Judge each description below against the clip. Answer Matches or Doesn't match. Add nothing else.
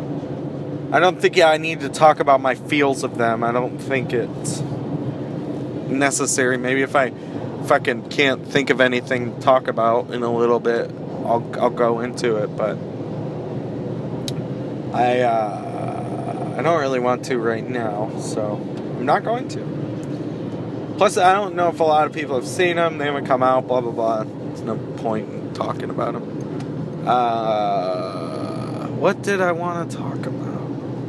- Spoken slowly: Doesn't match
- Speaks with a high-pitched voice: Doesn't match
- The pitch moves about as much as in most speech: Matches